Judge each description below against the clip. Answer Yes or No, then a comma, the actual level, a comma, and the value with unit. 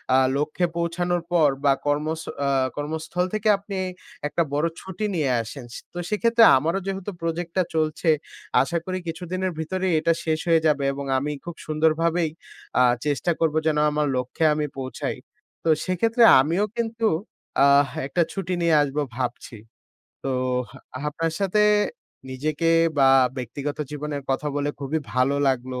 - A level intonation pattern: No, average, 3.7 semitones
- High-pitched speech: No, medium, 160 Hz